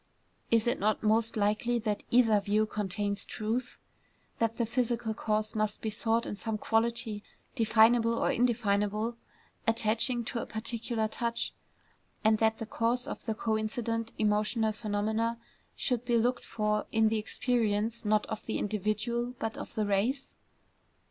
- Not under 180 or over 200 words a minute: No, average, 150 wpm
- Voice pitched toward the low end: No, high, 220 Hz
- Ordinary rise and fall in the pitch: No, narrow, 1.6 semitones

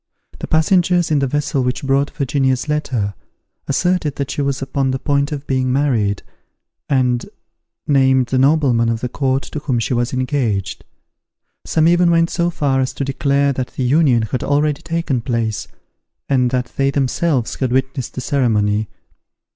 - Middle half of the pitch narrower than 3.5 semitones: Yes, narrow, 2.6 semitones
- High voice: No, low, 135 Hz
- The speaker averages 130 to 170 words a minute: Yes, average, 165 wpm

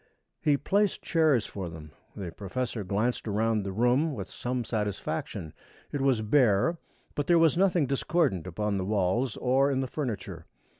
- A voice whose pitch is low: Yes, low, 120 Hz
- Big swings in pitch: Yes, wide, 6.1 semitones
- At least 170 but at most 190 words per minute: No, average, 160 wpm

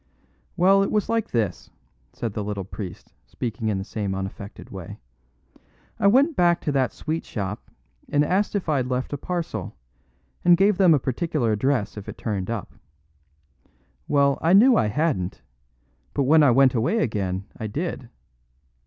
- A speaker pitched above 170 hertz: No, low, 130 Hz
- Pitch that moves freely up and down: Yes, wide, 8.5 semitones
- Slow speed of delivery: No, average, 165 wpm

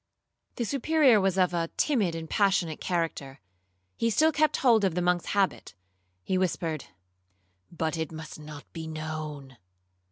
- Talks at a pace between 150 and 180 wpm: No, average, 140 wpm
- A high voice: No, medium, 170 Hz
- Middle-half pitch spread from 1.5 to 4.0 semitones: No, average, 4.4 semitones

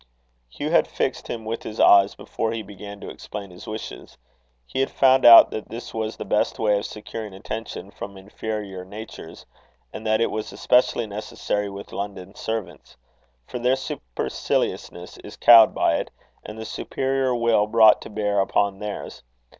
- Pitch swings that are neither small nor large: No, narrow, 2.1 semitones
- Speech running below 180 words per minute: Yes, average, 170 wpm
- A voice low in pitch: Yes, low, 105 Hz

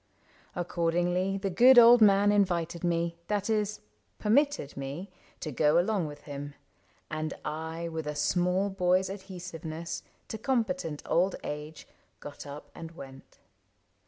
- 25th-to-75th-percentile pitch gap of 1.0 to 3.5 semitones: No, average, 4.1 semitones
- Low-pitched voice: No, medium, 175 Hz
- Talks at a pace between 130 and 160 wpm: Yes, average, 140 wpm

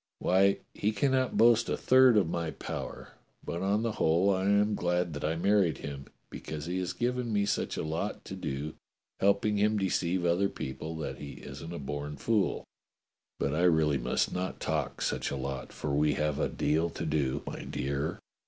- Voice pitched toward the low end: Yes, very low, 85 Hz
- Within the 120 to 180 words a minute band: No, average, 190 wpm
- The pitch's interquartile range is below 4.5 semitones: No, average, 5.2 semitones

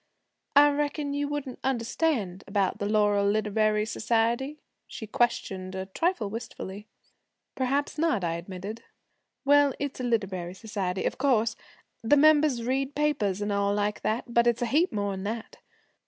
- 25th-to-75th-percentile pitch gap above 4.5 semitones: Yes, wide, 5.6 semitones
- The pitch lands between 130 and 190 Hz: No, high, 225 Hz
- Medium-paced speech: Yes, average, 150 wpm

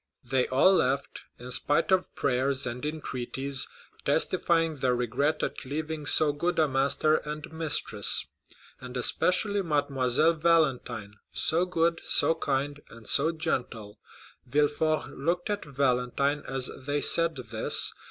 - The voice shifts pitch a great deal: No, average, 3.8 semitones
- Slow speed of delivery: Yes, slow, 130 wpm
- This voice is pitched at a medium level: Yes, medium, 145 Hz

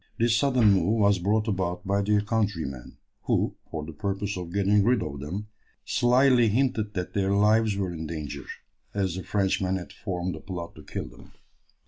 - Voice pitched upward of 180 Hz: No, low, 100 Hz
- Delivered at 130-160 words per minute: No, average, 180 wpm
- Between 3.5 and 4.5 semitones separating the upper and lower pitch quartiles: No, average, 3.1 semitones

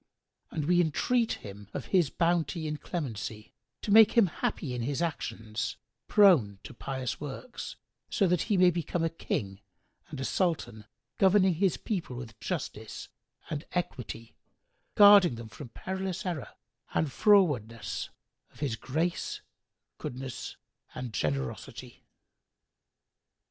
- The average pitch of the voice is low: No, medium, 155 Hz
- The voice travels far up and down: Yes, wide, 7.3 semitones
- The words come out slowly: Yes, slow, 125 wpm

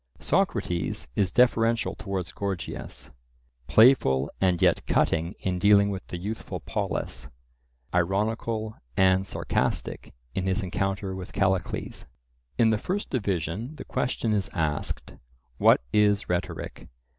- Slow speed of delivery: Yes, slow, 115 wpm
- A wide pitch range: No, average, 3.5 semitones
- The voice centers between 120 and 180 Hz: No, very low, 95 Hz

